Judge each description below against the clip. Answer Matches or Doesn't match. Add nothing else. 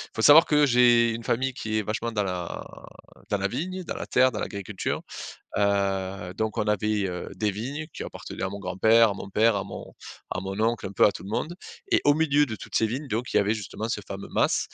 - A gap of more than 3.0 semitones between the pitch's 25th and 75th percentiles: Matches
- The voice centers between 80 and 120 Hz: Matches